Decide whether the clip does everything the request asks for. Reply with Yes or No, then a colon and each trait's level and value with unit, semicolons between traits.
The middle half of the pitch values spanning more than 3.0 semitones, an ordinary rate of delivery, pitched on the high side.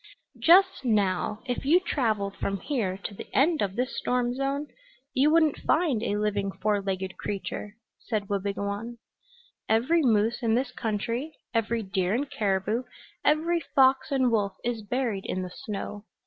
Yes: average, 4.8 semitones; average, 155 wpm; high, 225 Hz